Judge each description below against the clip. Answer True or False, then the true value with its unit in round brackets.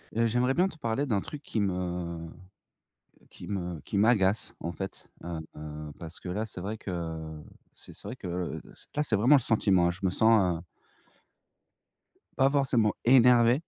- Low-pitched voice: True (100 Hz)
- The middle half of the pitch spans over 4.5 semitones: True (5.2 semitones)